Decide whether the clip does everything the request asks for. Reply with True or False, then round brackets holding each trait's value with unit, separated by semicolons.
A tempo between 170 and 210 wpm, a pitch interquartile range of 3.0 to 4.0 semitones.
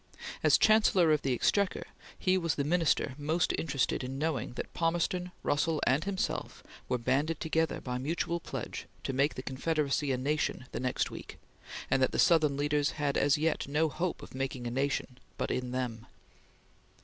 True (175 wpm; 3.7 semitones)